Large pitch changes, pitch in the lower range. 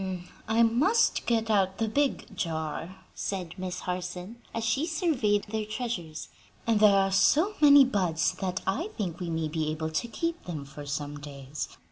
No: wide, 6.1 semitones; high, 195 Hz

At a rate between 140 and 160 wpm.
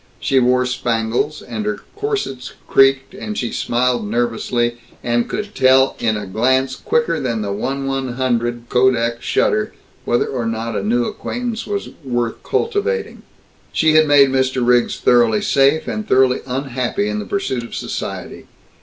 Yes: average, 150 wpm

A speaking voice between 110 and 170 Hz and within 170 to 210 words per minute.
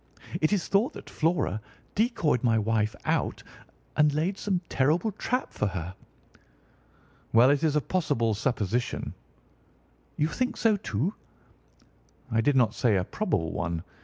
No: medium, 140 Hz; average, 140 wpm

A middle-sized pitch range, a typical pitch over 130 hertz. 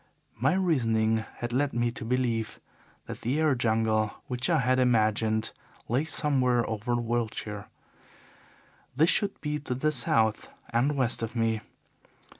No: average, 3.3 semitones; low, 120 Hz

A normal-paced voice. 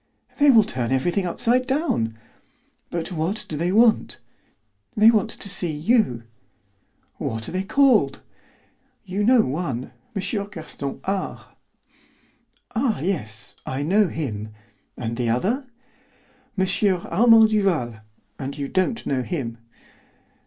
No: slow, 125 wpm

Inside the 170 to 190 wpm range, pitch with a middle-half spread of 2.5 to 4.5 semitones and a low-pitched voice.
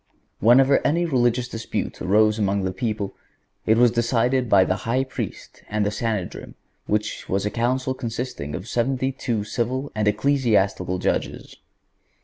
No: average, 145 wpm; average, 3.6 semitones; low, 115 Hz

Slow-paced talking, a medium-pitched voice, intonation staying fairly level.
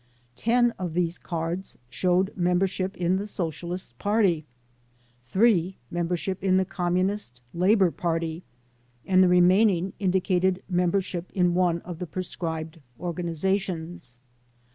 Yes: slow, 115 wpm; medium, 180 Hz; narrow, 1.9 semitones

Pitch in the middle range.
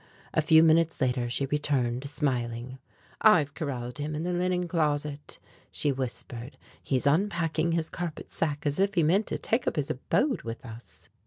Yes: medium, 150 Hz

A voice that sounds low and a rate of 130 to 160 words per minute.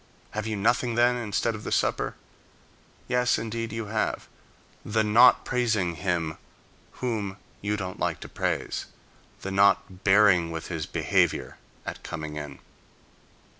Yes: low, 105 Hz; slow, 135 wpm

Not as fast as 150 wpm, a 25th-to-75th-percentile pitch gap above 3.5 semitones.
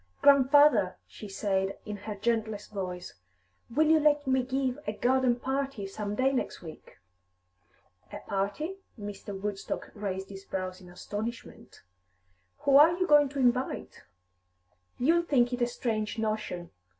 Yes: average, 140 wpm; average, 5.1 semitones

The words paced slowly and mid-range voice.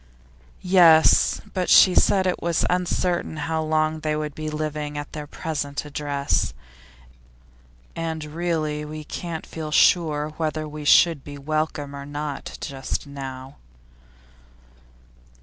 Yes: slow, 125 wpm; medium, 155 Hz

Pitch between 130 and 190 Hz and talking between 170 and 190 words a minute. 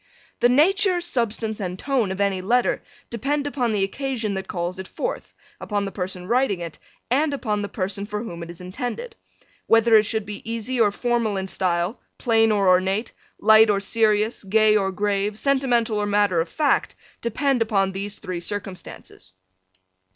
No: high, 210 Hz; average, 175 wpm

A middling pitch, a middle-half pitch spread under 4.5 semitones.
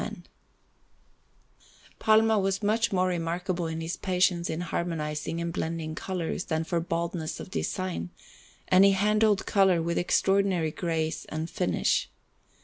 Yes: medium, 175 Hz; average, 2.8 semitones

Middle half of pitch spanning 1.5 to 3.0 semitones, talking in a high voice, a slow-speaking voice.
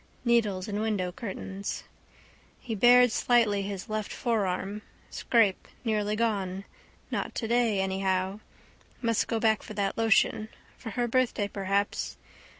Yes: average, 2.7 semitones; high, 210 Hz; slow, 125 wpm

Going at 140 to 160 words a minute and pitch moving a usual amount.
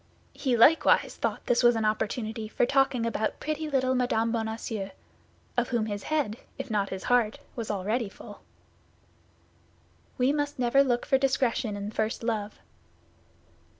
Yes: average, 150 wpm; average, 3.2 semitones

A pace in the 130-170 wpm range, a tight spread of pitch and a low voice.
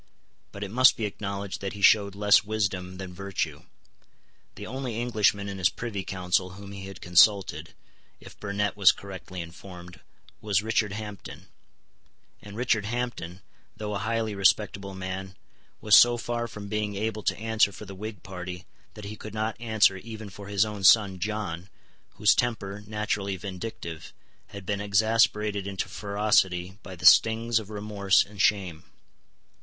Yes: average, 160 wpm; narrow, 2.1 semitones; low, 100 Hz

